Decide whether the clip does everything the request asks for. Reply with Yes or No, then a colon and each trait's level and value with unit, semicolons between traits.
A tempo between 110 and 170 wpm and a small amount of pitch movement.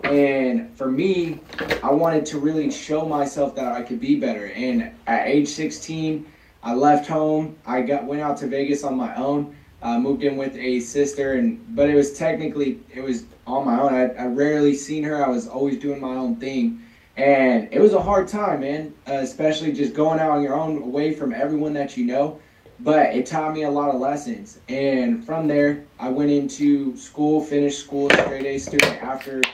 No: fast, 205 wpm; narrow, 2.2 semitones